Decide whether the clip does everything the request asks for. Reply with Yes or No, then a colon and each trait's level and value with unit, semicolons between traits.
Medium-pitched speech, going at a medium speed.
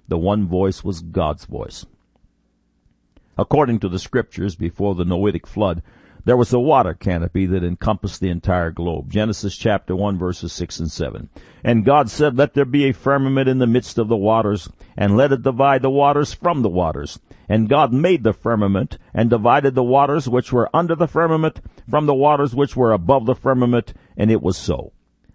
No: low, 110 Hz; average, 190 wpm